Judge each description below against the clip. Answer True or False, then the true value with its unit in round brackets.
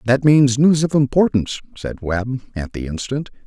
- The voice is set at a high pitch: False (125 Hz)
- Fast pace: False (175 wpm)